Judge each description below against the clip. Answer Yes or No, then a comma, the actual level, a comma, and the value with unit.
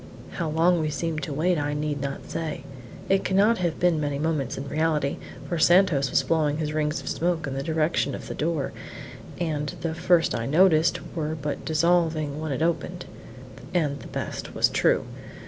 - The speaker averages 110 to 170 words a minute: No, average, 190 wpm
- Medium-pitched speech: Yes, medium, 155 Hz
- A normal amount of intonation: No, narrow, 2.3 semitones